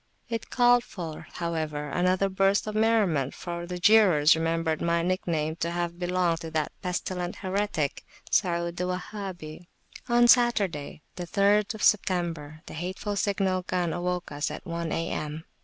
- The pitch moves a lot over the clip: No, average, 3.0 semitones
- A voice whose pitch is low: No, medium, 175 Hz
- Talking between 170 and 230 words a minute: No, average, 145 wpm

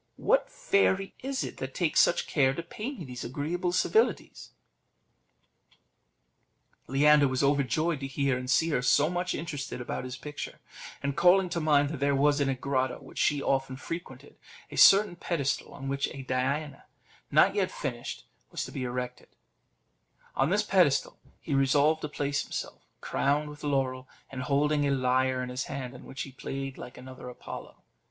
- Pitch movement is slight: No, average, 3.9 semitones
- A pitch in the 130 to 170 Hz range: Yes, medium, 140 Hz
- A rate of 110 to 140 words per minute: No, average, 175 wpm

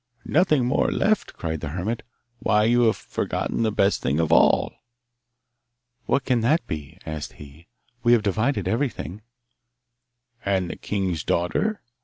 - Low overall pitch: Yes, low, 105 Hz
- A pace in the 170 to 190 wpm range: No, average, 145 wpm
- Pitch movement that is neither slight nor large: No, wide, 6.1 semitones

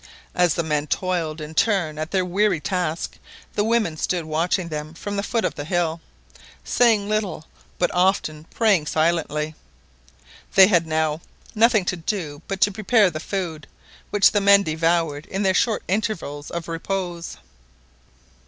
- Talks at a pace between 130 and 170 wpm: Yes, average, 155 wpm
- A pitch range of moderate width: Yes, average, 4.1 semitones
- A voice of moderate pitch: Yes, medium, 175 Hz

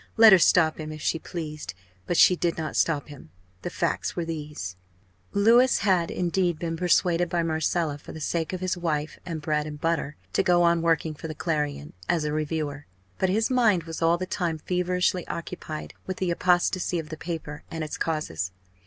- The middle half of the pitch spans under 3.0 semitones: Yes, narrow, 2.6 semitones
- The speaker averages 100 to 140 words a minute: No, average, 195 wpm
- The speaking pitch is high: No, medium, 165 Hz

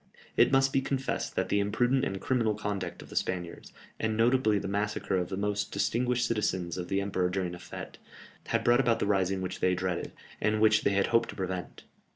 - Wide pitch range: No, average, 3.7 semitones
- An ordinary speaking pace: No, fast, 210 wpm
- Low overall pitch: Yes, low, 100 Hz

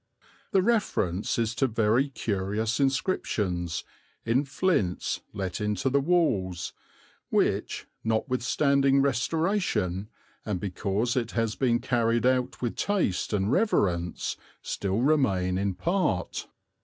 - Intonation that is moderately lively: No, wide, 5.9 semitones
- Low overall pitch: Yes, low, 115 Hz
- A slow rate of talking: Yes, slow, 110 wpm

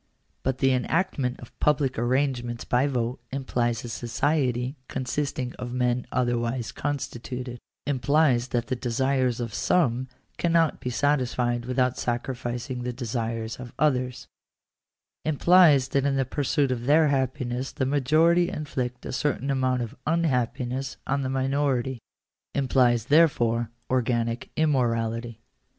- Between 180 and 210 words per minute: No, slow, 135 wpm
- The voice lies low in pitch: Yes, low, 130 Hz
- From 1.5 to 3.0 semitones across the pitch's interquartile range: Yes, narrow, 2.5 semitones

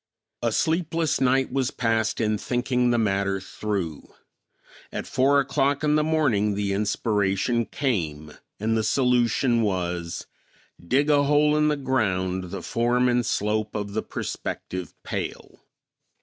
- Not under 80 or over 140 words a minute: Yes, slow, 135 wpm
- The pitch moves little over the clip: No, average, 5.1 semitones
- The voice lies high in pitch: No, low, 115 Hz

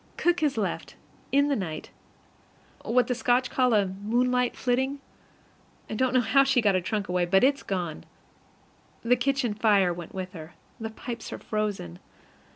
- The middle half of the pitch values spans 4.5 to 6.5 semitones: Yes, average, 4.8 semitones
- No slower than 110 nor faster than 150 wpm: No, average, 165 wpm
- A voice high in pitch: Yes, high, 225 Hz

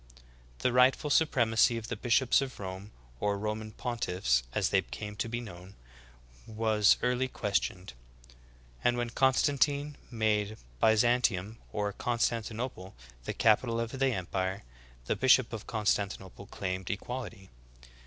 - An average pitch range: Yes, average, 3.5 semitones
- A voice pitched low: Yes, low, 110 Hz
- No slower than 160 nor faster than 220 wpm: No, slow, 135 wpm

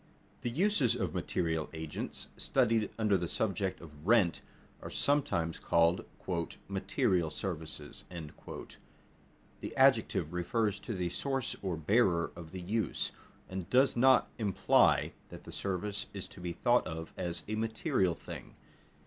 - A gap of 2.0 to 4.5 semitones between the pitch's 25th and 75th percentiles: No, average, 5.3 semitones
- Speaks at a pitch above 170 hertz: No, very low, 95 Hz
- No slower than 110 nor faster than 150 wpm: Yes, average, 140 wpm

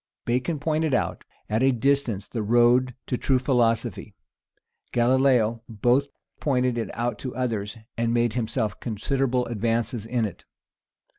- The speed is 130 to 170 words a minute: Yes, slow, 135 wpm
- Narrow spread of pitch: Yes, narrow, 2.2 semitones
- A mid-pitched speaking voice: No, low, 120 Hz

